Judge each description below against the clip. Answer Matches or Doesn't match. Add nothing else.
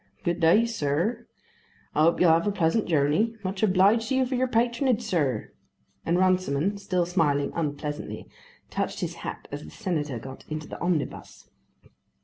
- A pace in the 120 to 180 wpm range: Matches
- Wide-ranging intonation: Matches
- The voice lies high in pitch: Doesn't match